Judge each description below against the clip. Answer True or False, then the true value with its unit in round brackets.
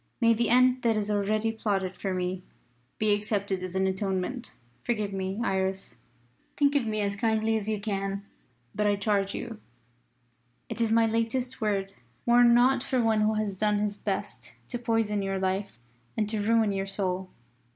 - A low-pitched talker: False (210 Hz)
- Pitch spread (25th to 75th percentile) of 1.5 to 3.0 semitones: True (2.6 semitones)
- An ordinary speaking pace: True (175 wpm)